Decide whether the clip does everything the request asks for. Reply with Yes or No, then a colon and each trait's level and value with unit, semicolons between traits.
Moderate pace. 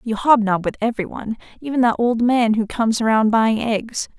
Yes: average, 185 wpm